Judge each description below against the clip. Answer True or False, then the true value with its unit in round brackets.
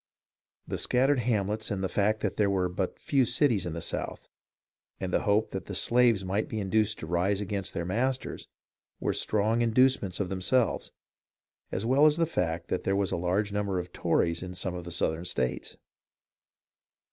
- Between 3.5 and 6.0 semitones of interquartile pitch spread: True (3.9 semitones)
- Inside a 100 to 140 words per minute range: False (185 wpm)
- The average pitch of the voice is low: True (100 Hz)